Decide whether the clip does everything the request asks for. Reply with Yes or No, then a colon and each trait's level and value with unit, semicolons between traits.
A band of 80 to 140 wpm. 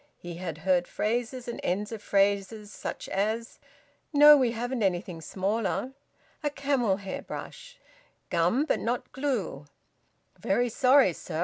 Yes: slow, 135 wpm